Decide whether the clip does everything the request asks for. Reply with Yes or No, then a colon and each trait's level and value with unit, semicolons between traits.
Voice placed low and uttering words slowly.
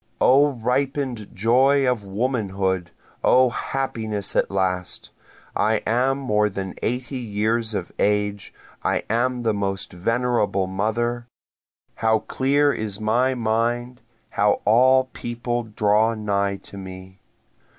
Yes: low, 110 Hz; slow, 120 wpm